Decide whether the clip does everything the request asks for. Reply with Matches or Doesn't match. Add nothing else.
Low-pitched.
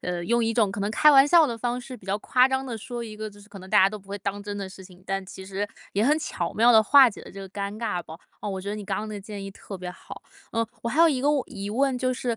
Doesn't match